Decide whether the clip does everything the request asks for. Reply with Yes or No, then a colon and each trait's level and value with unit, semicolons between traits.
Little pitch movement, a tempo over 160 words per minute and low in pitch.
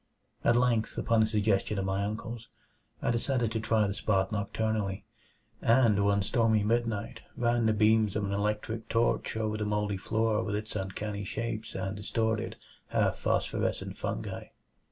No: narrow, 1.8 semitones; average, 155 wpm; low, 110 Hz